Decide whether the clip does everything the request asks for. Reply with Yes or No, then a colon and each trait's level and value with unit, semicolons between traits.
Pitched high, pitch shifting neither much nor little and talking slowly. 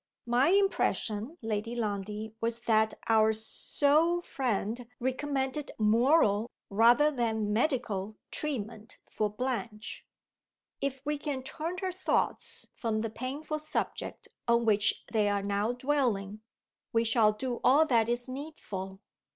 Yes: high, 235 Hz; average, 4.4 semitones; slow, 125 wpm